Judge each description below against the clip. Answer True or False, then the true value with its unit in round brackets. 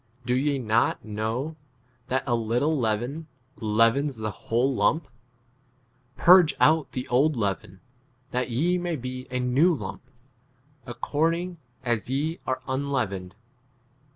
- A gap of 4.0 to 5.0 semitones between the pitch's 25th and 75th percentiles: True (4.7 semitones)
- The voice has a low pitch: True (130 Hz)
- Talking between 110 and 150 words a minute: True (135 wpm)